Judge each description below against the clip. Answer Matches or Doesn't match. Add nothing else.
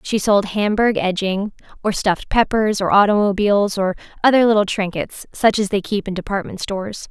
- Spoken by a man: Doesn't match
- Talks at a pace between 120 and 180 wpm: Matches